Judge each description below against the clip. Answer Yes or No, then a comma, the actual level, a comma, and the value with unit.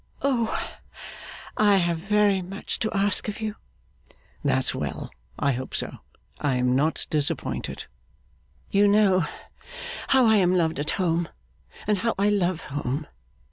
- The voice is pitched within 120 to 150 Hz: No, high, 190 Hz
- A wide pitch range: No, average, 4.6 semitones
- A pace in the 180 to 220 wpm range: No, average, 140 wpm